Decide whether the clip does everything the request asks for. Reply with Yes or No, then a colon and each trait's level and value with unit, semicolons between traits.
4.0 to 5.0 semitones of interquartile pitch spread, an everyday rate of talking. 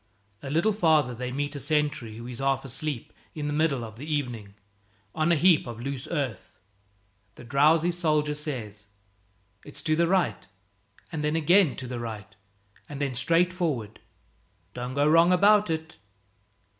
Yes: average, 4.5 semitones; average, 165 wpm